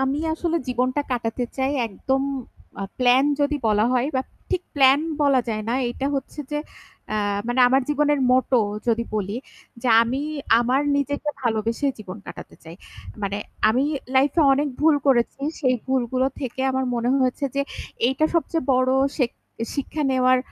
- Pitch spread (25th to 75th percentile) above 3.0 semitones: No, average, 2.7 semitones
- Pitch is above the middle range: Yes, very high, 260 Hz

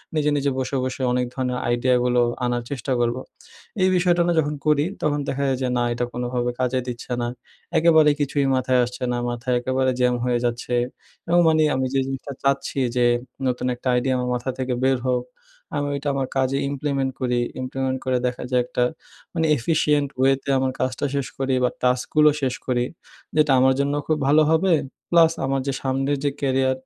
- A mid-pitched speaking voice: No, low, 130 Hz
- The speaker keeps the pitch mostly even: Yes, narrow, 2.3 semitones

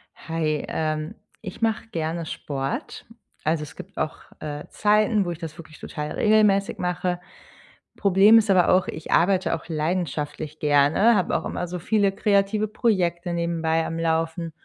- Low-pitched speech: No, medium, 170 Hz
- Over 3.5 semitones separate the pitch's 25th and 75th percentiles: Yes, average, 4.0 semitones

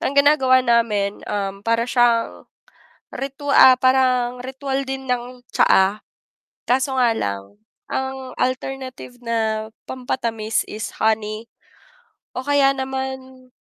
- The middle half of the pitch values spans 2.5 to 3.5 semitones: Yes, average, 2.8 semitones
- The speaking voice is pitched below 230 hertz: No, very high, 255 Hz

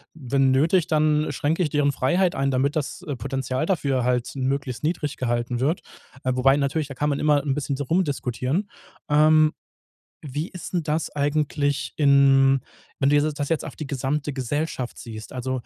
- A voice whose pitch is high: No, medium, 145 Hz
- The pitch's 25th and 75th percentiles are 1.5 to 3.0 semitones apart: Yes, narrow, 2.5 semitones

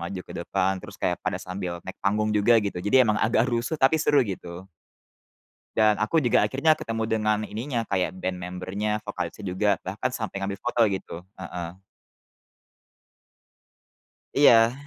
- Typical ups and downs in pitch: Yes, average, 3.7 semitones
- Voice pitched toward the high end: No, low, 105 Hz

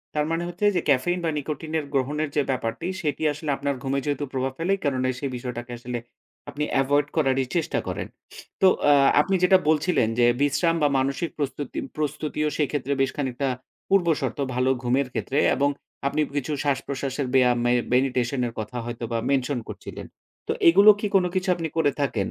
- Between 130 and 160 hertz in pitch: Yes, medium, 140 Hz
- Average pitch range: Yes, average, 3.2 semitones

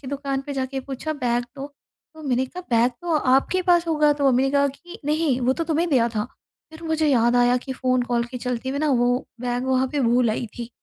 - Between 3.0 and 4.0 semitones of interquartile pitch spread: Yes, average, 3.4 semitones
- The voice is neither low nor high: No, very high, 265 Hz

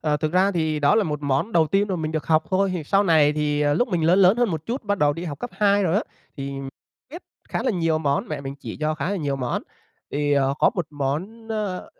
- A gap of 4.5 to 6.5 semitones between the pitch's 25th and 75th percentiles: Yes, average, 5.0 semitones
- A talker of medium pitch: Yes, medium, 160 Hz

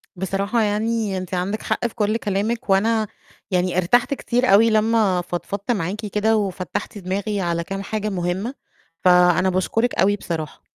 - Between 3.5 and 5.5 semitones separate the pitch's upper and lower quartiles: No, average, 3.1 semitones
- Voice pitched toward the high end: Yes, high, 200 Hz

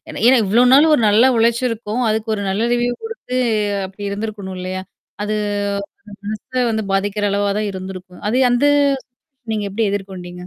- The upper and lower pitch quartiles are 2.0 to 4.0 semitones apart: Yes, average, 3.3 semitones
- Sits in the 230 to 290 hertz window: No, high, 210 Hz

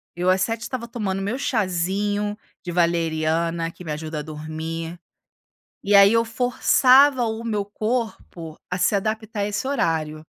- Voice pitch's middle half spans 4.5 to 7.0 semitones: Yes, average, 5.2 semitones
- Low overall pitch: No, high, 195 Hz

